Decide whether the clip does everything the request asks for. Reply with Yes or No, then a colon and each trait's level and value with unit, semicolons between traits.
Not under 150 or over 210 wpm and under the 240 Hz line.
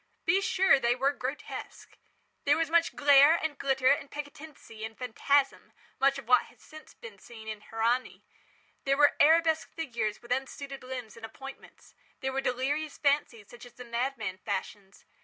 No: average, 160 wpm; very high, 270 Hz